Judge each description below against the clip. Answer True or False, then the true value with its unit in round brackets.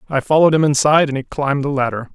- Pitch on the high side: False (140 Hz)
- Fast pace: True (250 wpm)